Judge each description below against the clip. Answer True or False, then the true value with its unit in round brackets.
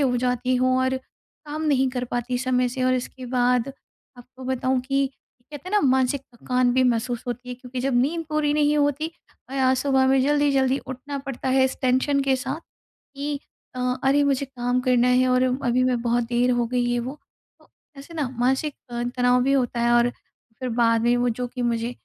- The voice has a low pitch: False (255 Hz)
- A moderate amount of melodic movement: False (1.7 semitones)